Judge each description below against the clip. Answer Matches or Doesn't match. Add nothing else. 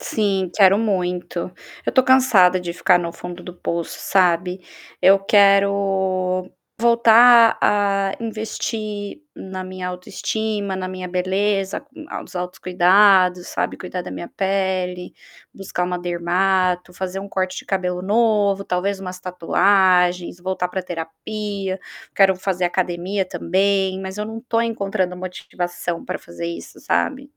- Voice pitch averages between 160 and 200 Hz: Matches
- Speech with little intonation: Matches